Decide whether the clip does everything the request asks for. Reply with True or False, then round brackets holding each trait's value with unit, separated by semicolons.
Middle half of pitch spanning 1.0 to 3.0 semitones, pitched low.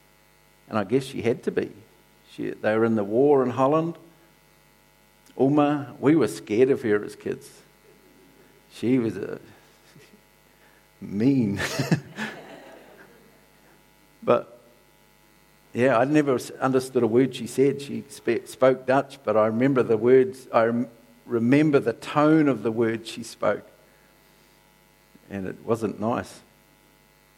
False (3.5 semitones; 130 Hz)